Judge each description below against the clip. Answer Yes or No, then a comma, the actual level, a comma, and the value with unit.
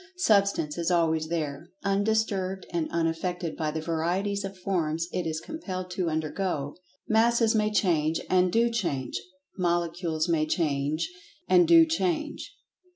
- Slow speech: Yes, slow, 125 wpm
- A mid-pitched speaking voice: Yes, medium, 175 Hz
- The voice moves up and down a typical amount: Yes, average, 3.5 semitones